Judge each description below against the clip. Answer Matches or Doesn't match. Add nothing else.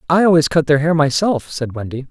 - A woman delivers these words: Doesn't match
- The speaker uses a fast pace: Matches